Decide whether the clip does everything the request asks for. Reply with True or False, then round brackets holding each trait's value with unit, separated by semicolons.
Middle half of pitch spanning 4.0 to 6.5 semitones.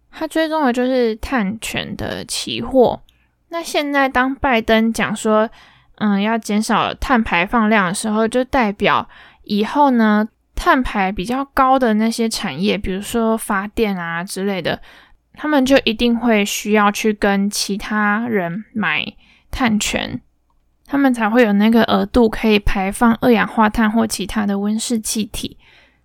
False (3.2 semitones)